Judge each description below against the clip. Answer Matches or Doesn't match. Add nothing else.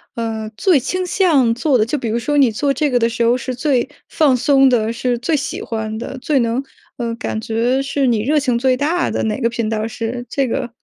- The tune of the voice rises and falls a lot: Doesn't match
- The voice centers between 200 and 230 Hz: Doesn't match